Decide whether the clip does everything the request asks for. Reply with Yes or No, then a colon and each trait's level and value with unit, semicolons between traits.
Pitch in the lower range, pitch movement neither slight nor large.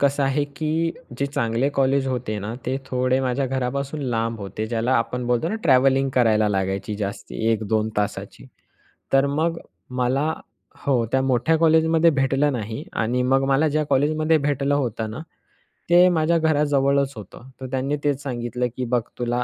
Yes: low, 130 Hz; average, 3.3 semitones